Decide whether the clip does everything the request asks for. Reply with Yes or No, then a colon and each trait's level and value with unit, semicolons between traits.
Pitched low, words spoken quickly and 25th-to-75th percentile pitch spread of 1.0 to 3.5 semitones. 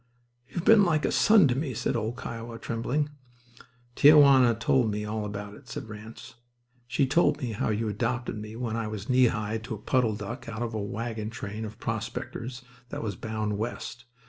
No: low, 115 Hz; average, 195 wpm; average, 2.9 semitones